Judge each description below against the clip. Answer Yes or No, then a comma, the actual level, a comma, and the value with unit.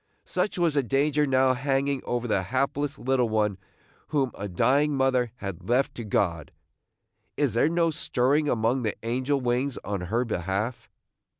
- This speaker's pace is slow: No, average, 160 wpm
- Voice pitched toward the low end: Yes, low, 125 Hz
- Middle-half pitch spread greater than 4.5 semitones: No, average, 3.9 semitones